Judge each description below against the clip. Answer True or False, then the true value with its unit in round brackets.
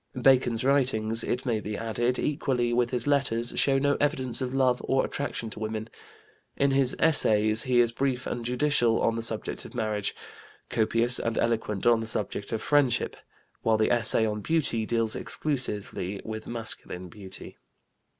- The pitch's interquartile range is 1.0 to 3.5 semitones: True (2.9 semitones)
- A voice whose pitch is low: True (120 Hz)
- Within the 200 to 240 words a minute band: False (165 wpm)